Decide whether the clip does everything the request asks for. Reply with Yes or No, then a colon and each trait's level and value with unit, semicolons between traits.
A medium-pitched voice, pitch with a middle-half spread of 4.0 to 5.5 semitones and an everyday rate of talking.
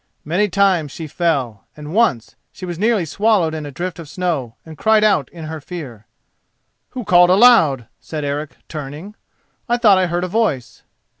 Yes: medium, 170 Hz; average, 5.0 semitones; average, 175 wpm